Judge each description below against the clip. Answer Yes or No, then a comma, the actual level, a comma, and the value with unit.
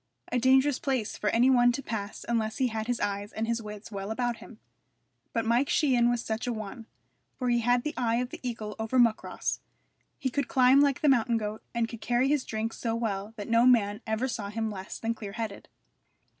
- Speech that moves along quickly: Yes, fast, 220 wpm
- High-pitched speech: Yes, high, 230 Hz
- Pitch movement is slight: Yes, narrow, 2.3 semitones